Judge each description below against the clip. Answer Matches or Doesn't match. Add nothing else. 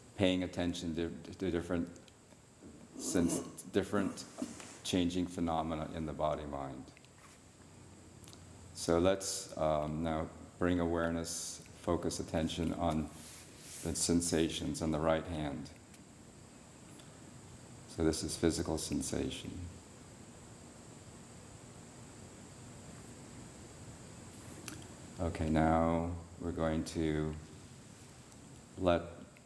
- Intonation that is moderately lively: Doesn't match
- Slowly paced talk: Matches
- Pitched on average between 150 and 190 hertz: Doesn't match